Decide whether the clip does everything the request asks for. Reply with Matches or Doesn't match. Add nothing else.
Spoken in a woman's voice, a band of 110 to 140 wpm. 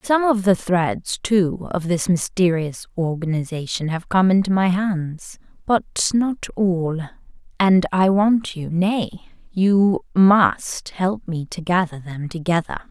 Matches